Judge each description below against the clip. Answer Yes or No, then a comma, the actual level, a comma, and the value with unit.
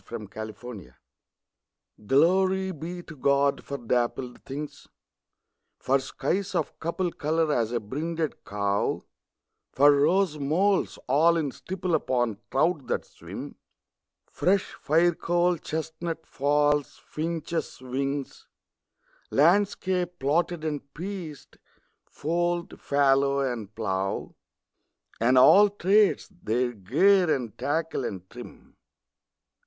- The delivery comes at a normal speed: No, slow, 105 wpm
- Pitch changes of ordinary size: Yes, average, 5.0 semitones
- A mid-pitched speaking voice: Yes, medium, 150 Hz